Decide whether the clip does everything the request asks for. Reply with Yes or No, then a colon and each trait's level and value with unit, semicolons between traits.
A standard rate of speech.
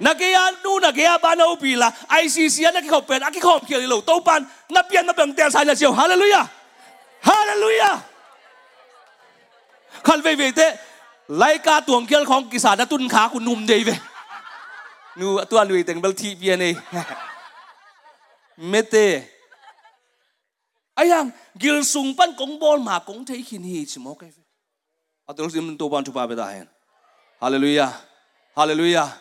No: slow, 70 wpm